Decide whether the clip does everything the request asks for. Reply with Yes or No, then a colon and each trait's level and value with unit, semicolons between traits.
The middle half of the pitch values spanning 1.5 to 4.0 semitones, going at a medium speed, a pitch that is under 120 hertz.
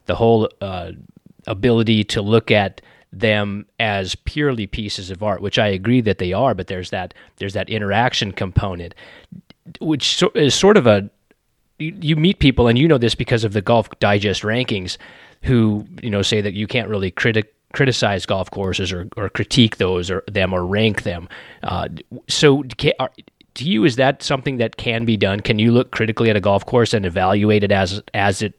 Yes: average, 3.3 semitones; average, 195 wpm; low, 110 Hz